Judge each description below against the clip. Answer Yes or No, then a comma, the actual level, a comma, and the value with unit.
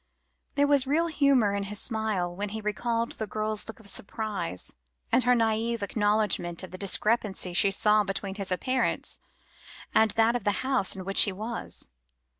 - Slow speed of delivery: No, average, 175 wpm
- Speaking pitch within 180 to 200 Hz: No, high, 215 Hz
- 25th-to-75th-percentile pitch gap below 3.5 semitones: Yes, average, 2.8 semitones